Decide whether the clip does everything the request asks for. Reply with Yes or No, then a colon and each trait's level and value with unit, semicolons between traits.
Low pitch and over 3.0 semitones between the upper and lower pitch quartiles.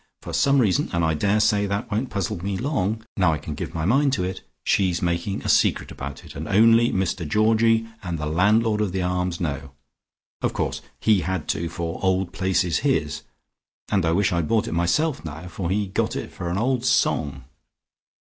Yes: very low, 95 Hz; average, 4.2 semitones